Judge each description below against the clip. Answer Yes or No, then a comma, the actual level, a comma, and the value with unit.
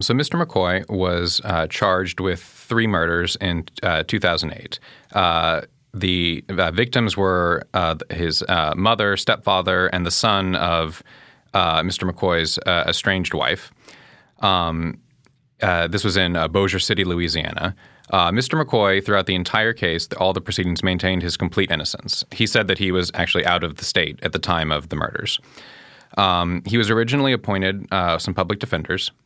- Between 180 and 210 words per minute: No, average, 165 wpm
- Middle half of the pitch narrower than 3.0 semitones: Yes, narrow, 2.5 semitones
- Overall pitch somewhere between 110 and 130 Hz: No, very low, 95 Hz